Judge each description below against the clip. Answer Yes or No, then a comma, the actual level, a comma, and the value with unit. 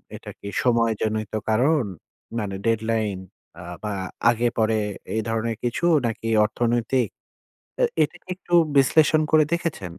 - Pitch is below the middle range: Yes, low, 115 Hz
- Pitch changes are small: No, average, 3.2 semitones